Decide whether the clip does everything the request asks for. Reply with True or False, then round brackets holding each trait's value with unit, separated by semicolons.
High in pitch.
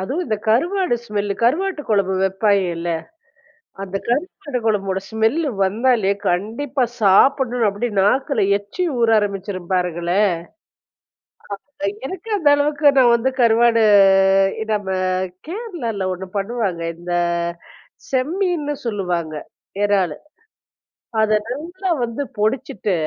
True (220 Hz)